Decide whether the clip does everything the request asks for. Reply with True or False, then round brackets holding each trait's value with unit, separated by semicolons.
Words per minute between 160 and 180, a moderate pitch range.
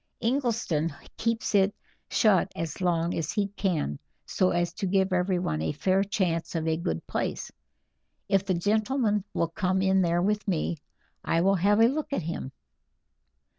True (165 wpm; 3.6 semitones)